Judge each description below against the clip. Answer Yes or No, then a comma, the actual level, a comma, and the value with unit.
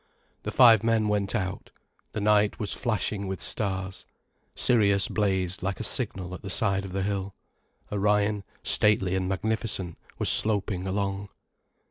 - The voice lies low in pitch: Yes, low, 100 Hz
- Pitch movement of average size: No, narrow, 1.8 semitones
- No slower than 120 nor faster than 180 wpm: Yes, average, 145 wpm